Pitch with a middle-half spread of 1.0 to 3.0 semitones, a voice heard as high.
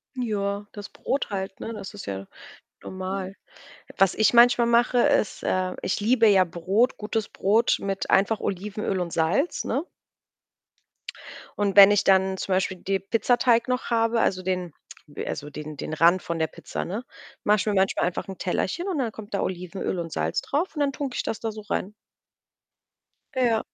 No: average, 3.6 semitones; high, 200 Hz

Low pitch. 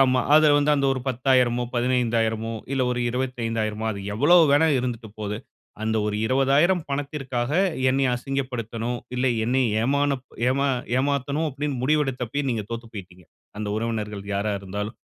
Yes: low, 125 Hz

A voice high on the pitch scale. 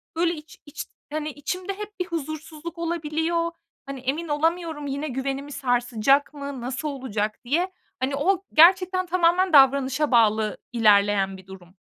Yes: very high, 290 Hz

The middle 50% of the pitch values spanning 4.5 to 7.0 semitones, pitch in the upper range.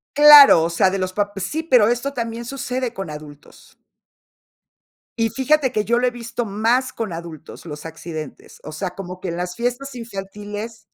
Yes: wide, 5.5 semitones; high, 215 Hz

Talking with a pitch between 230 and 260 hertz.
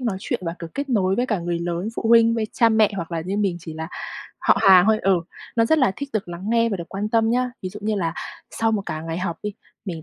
No: high, 200 Hz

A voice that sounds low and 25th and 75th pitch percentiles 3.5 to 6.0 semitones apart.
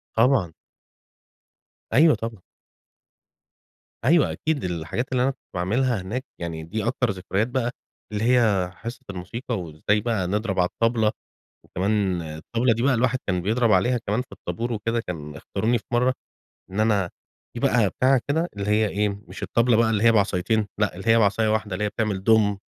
Yes: low, 110 Hz; average, 3.9 semitones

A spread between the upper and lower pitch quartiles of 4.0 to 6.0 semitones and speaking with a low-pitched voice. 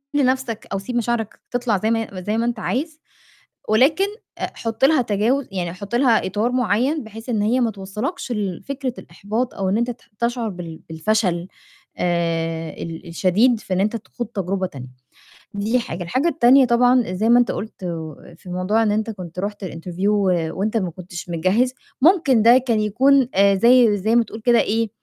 No: average, 4.6 semitones; high, 215 Hz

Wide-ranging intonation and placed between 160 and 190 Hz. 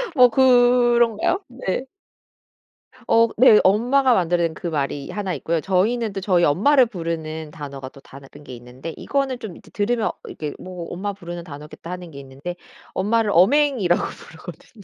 Yes: wide, 6.7 semitones; medium, 185 Hz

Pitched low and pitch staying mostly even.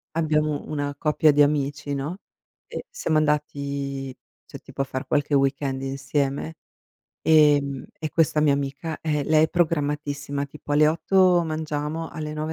No: medium, 150 Hz; narrow, 1.7 semitones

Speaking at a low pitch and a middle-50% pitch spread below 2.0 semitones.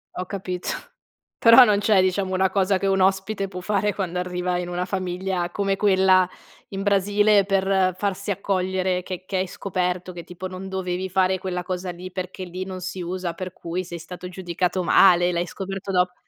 No: medium, 185 Hz; narrow, 1.3 semitones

